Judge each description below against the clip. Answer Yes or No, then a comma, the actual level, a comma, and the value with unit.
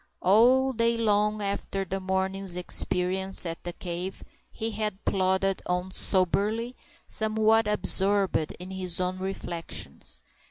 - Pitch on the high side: Yes, high, 195 Hz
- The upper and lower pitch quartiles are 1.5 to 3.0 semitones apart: Yes, narrow, 2.6 semitones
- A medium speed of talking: No, slow, 120 wpm